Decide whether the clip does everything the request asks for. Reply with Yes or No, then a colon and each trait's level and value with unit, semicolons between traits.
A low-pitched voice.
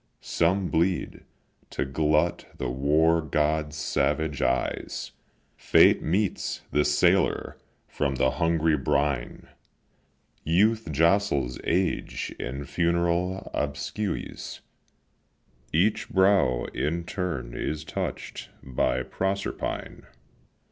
Yes: very low, 80 Hz